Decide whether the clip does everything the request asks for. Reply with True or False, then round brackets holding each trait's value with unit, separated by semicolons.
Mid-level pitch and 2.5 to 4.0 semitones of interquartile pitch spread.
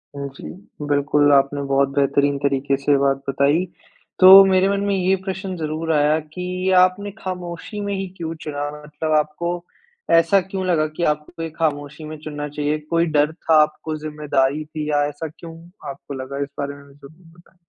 True (155 Hz; 3.3 semitones)